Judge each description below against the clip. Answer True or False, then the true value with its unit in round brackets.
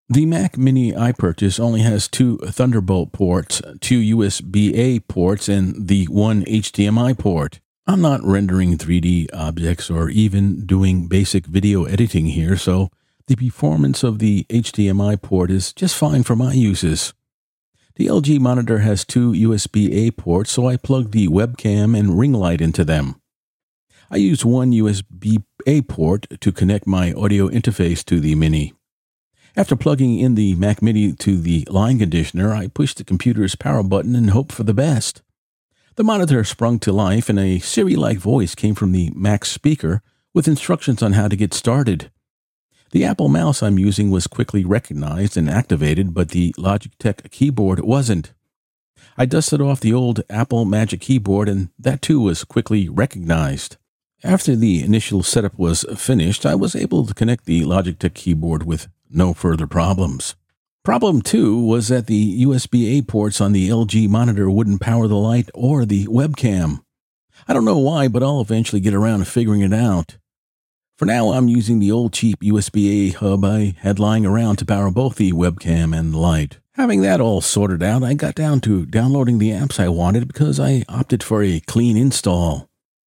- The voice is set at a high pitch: False (105 Hz)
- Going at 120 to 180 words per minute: True (175 wpm)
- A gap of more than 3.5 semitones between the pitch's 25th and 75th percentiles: True (4.2 semitones)